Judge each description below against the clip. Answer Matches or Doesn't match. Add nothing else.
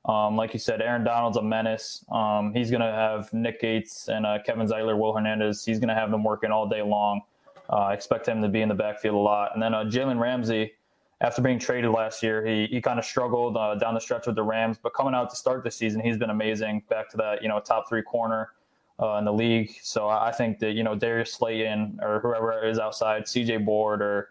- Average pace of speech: Doesn't match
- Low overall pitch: Matches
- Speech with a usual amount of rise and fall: Doesn't match